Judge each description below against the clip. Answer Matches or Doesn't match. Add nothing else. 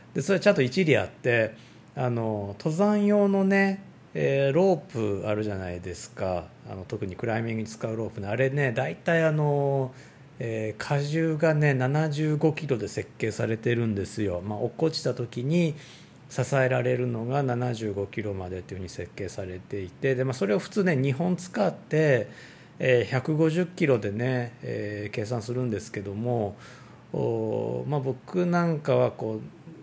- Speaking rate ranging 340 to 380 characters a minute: Doesn't match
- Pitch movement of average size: Doesn't match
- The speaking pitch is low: Matches